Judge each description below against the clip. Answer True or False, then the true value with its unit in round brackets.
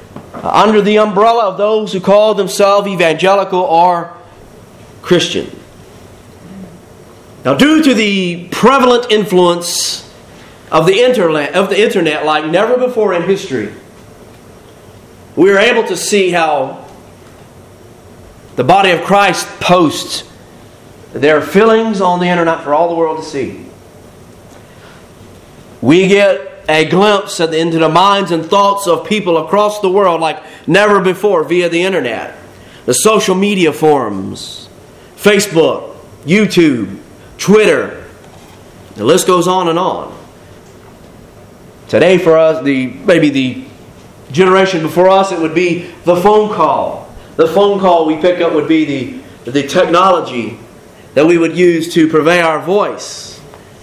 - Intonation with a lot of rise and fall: False (4.0 semitones)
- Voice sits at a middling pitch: True (180 Hz)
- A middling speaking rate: False (130 wpm)